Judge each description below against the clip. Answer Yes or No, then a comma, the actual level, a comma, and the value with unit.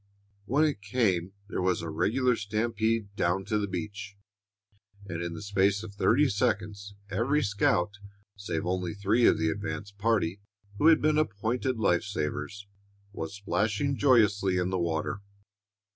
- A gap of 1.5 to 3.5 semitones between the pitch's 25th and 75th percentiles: Yes, average, 3.2 semitones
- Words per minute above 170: No, average, 150 wpm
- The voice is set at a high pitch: No, low, 100 Hz